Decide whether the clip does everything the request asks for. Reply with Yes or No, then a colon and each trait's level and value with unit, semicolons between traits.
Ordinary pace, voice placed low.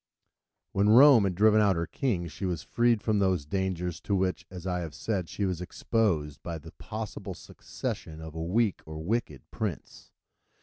Yes: average, 180 wpm; very low, 95 Hz